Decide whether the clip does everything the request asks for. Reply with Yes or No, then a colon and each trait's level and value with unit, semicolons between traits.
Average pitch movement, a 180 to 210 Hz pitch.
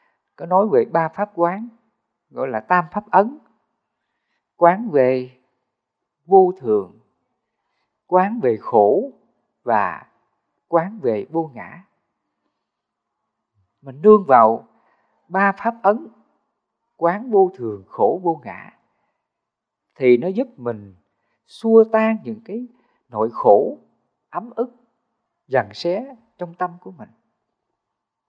No: wide, 5.7 semitones; high, 190 Hz